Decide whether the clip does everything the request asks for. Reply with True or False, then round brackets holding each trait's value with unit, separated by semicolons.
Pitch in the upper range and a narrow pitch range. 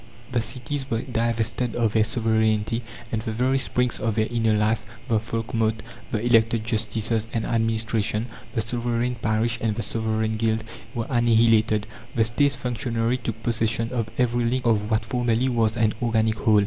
False (115 Hz; 1.4 semitones)